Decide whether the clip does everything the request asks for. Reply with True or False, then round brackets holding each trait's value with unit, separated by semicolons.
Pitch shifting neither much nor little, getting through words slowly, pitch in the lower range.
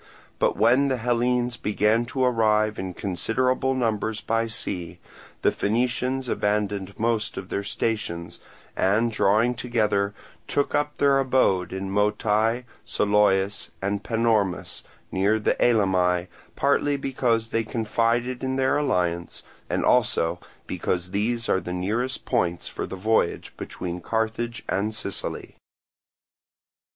True (3.6 semitones; 125 wpm; 110 Hz)